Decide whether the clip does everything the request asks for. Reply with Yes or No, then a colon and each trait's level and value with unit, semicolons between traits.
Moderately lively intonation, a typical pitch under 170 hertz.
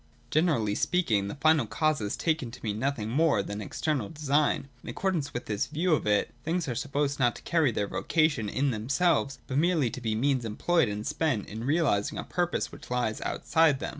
No: wide, 6.1 semitones; medium, 140 Hz